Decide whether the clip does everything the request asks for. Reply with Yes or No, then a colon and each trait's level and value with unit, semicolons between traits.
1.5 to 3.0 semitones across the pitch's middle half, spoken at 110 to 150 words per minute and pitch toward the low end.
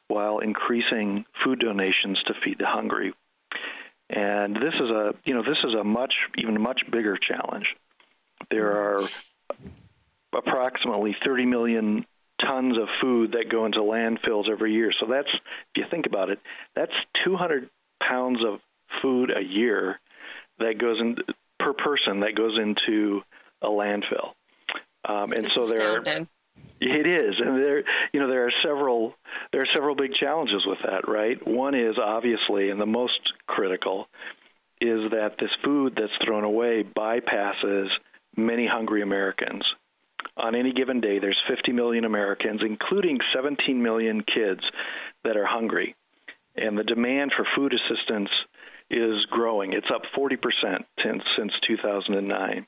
Yes: narrow, 2.5 semitones; average, 145 wpm; low, 110 Hz